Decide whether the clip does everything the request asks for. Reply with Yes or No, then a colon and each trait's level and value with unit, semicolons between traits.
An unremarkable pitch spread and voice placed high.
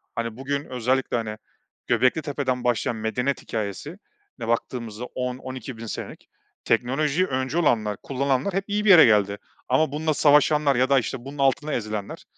No: average, 3.7 semitones; low, 130 Hz